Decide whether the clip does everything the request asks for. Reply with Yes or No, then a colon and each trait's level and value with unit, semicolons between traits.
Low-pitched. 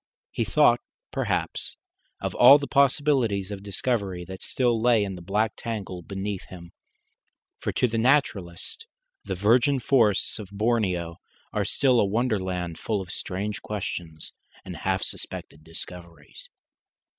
Yes: low, 100 Hz